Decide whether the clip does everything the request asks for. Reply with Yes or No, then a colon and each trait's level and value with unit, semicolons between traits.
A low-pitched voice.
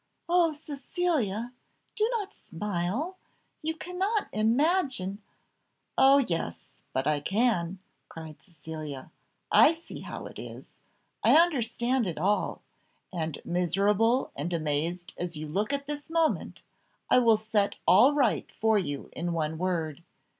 No: high, 210 Hz